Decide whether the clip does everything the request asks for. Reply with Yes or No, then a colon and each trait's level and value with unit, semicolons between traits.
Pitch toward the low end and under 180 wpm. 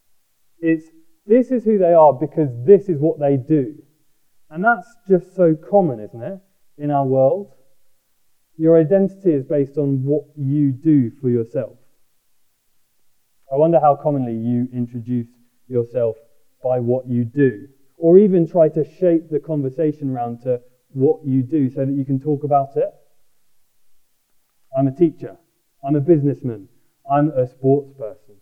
No: medium, 145 Hz; average, 150 wpm